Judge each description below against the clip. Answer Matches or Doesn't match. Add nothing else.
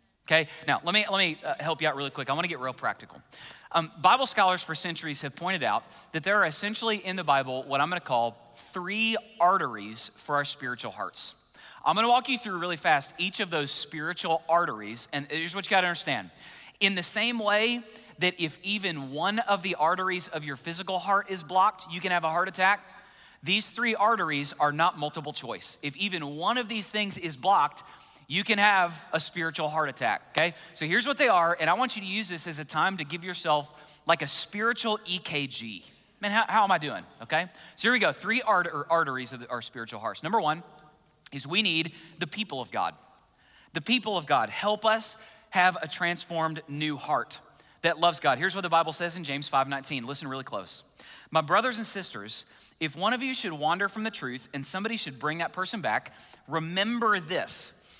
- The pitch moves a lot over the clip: Doesn't match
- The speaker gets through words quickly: Matches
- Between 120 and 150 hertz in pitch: Doesn't match